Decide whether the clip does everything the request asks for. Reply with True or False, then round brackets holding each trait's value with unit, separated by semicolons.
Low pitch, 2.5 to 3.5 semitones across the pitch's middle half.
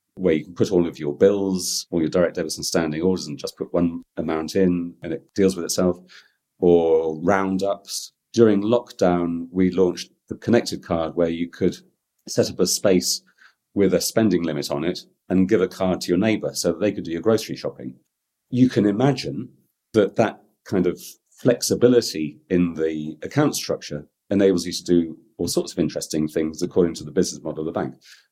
True (90 Hz; 3.1 semitones)